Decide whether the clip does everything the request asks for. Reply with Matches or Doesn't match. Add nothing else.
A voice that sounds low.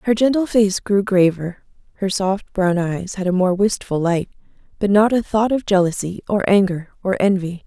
Doesn't match